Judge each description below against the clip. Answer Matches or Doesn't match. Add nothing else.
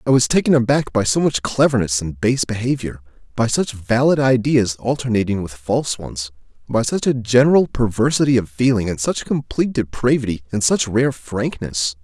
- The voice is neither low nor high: Doesn't match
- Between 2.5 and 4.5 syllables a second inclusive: Doesn't match